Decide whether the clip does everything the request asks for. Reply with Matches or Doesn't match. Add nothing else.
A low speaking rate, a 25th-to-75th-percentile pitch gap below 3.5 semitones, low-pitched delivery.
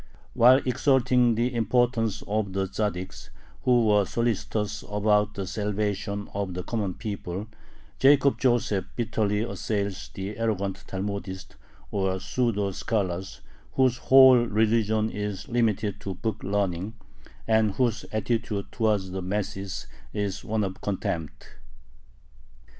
Matches